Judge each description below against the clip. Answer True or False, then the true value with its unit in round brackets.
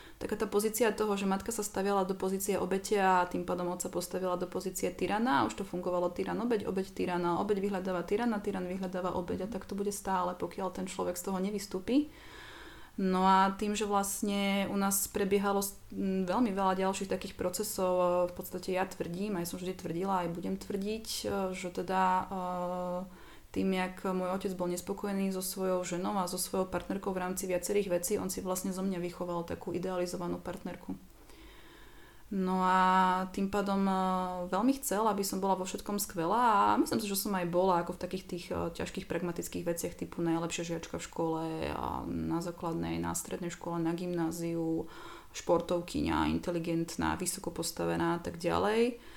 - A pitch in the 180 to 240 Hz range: True (185 Hz)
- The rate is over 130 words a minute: True (165 wpm)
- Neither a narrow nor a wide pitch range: False (2.1 semitones)